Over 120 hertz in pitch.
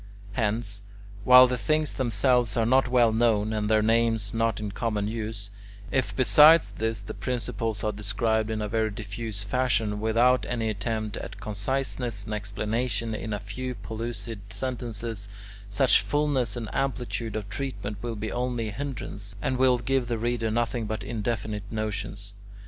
No: low, 115 Hz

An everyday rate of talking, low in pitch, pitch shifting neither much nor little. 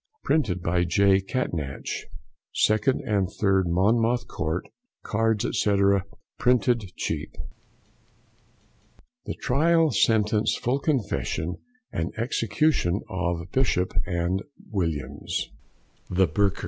No: slow, 95 wpm; low, 100 Hz; average, 5.0 semitones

